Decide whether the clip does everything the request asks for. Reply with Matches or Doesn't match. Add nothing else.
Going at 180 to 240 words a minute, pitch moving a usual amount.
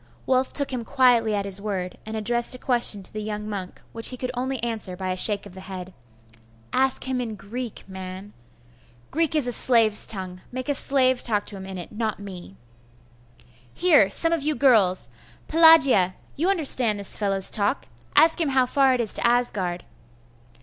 Matches